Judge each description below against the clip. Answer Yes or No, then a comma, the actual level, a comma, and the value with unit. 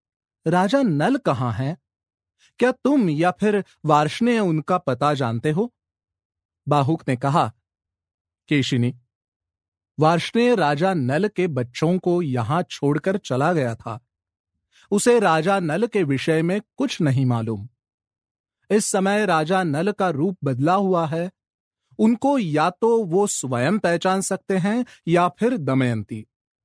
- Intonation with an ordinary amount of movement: No, wide, 8.3 semitones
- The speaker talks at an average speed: Yes, average, 130 wpm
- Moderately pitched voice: Yes, medium, 155 Hz